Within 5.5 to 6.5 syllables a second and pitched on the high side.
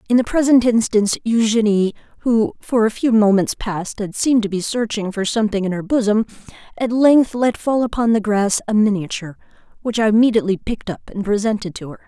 Yes: 5.9 syllables/s; high, 215 Hz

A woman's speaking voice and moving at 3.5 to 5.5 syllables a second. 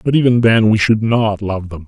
No: male; 5.1 syllables/s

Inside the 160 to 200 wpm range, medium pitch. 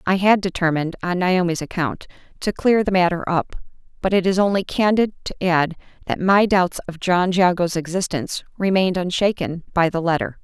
Yes: average, 170 wpm; medium, 180 Hz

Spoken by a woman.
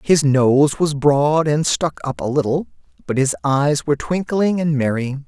No: male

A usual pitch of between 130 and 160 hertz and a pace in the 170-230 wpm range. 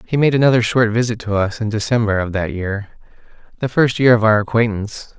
No: low, 110 Hz; average, 195 wpm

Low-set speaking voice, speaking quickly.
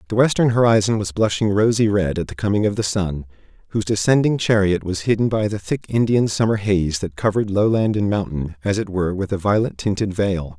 Yes: low, 100 Hz; fast, 210 wpm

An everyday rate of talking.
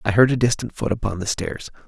No: fast, 255 wpm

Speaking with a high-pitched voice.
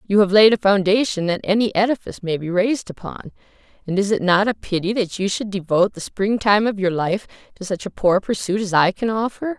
Yes: high, 200 Hz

